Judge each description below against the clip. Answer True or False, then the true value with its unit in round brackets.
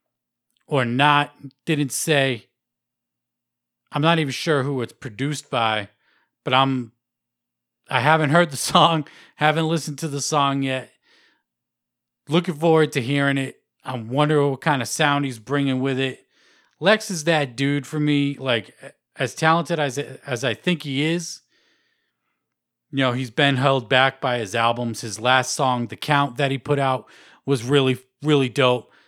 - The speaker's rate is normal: True (160 wpm)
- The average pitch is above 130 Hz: True (140 Hz)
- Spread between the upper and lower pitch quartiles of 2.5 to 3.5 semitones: True (3.2 semitones)